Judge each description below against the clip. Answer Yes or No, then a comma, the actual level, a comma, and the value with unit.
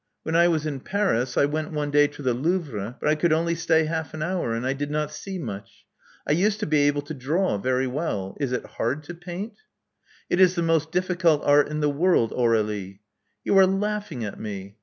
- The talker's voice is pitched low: No, medium, 150 Hz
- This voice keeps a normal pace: No, fast, 225 wpm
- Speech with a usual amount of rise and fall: Yes, average, 5.0 semitones